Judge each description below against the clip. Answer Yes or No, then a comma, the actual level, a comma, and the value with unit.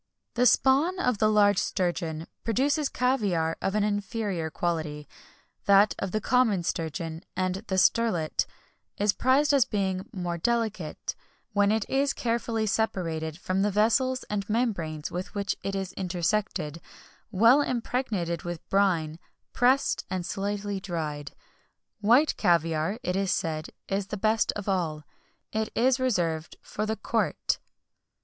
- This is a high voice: Yes, high, 200 Hz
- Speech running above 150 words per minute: No, average, 140 wpm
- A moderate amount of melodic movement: Yes, average, 4.8 semitones